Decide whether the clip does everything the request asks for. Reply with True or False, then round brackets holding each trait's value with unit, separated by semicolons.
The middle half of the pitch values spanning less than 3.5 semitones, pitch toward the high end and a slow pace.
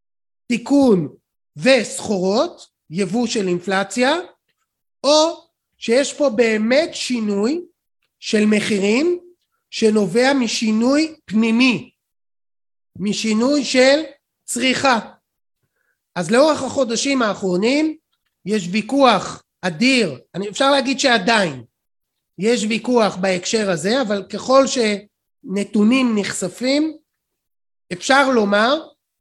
False (5.1 semitones; 235 Hz; 80 wpm)